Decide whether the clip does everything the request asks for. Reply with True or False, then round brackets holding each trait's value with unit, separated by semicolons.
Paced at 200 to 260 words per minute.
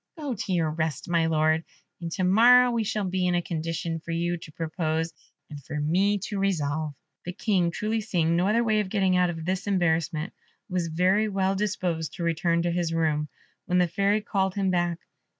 True (205 wpm)